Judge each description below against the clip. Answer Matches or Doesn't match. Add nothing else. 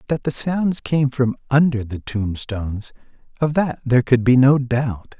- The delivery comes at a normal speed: Matches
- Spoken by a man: Matches